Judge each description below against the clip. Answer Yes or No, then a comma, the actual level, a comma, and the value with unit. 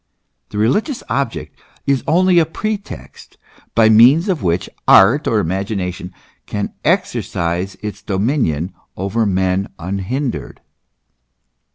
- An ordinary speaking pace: No, slow, 105 wpm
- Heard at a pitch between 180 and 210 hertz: No, low, 105 Hz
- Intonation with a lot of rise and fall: Yes, wide, 6.8 semitones